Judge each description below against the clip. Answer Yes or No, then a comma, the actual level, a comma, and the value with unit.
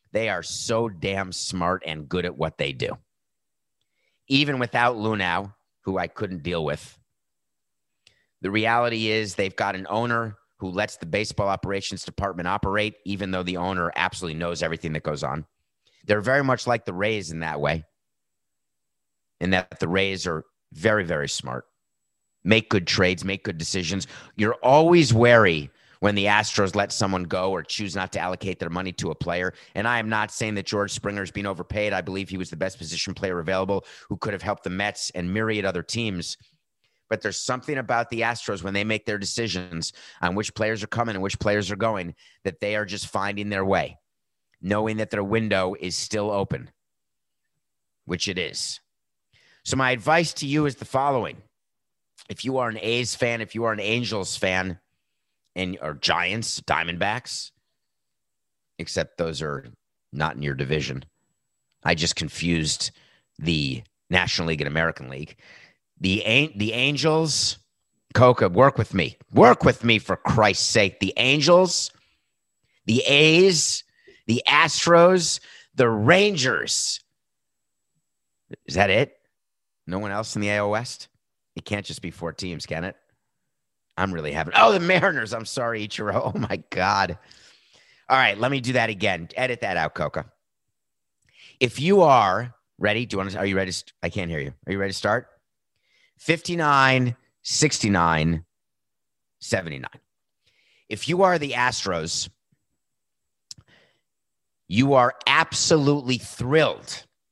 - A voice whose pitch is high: No, low, 105 Hz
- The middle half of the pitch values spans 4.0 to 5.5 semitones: Yes, average, 4.4 semitones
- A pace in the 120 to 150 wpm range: No, average, 160 wpm